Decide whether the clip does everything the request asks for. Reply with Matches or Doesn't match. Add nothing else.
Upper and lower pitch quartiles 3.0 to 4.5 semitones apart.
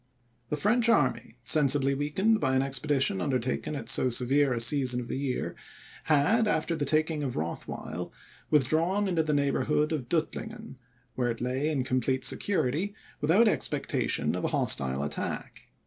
Matches